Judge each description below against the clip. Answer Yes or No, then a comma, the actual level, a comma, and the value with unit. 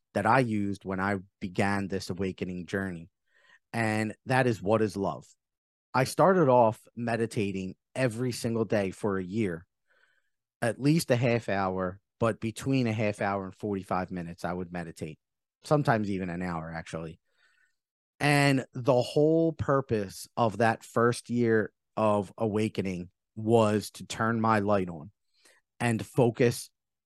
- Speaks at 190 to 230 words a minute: No, average, 140 wpm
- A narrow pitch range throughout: No, average, 3.8 semitones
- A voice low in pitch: Yes, low, 105 Hz